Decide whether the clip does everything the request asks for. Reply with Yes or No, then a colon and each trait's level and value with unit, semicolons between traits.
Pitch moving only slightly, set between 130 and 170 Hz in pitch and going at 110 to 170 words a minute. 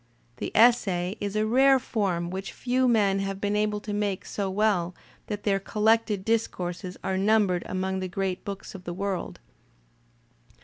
No: narrow, 2.3 semitones; high, 200 Hz; average, 165 wpm